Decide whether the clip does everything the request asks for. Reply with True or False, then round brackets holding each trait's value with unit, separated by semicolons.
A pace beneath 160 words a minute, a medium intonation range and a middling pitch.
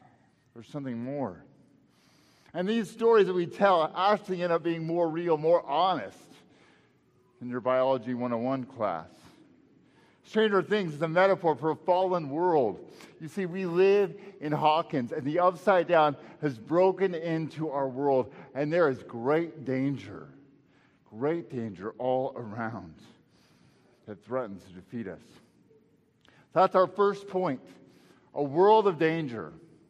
False (140 wpm; 5.8 semitones; 155 Hz)